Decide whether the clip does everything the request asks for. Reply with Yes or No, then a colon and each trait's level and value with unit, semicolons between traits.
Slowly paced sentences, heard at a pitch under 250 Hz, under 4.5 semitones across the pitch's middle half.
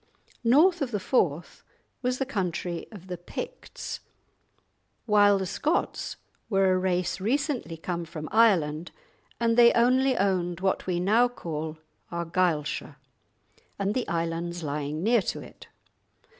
No: slow, 130 wpm; medium, 185 Hz; wide, 5.4 semitones